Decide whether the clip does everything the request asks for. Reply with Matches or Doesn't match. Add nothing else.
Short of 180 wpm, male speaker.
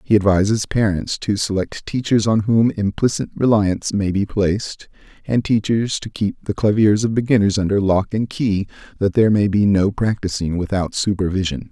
Matches